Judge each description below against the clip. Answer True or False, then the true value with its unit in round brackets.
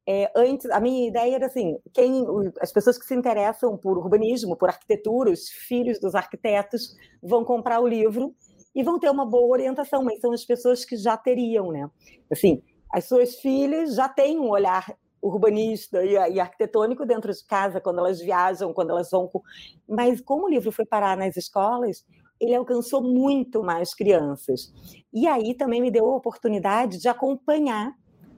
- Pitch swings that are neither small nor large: True (3.9 semitones)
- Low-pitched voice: False (235 Hz)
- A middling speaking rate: True (170 wpm)